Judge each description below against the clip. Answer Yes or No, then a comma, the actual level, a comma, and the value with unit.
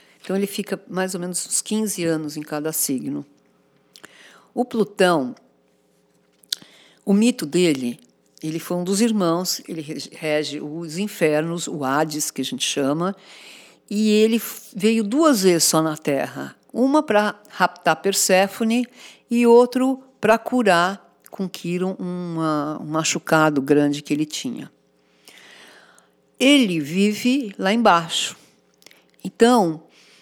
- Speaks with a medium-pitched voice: Yes, medium, 180 Hz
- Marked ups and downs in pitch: Yes, wide, 5.7 semitones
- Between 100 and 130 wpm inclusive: Yes, slow, 120 wpm